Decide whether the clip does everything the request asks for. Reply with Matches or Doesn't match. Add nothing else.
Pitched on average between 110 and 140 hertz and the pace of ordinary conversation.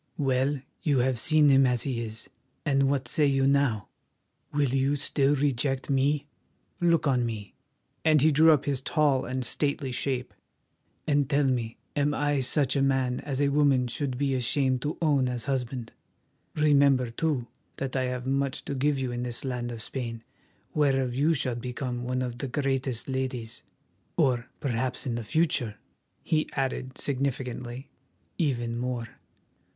Matches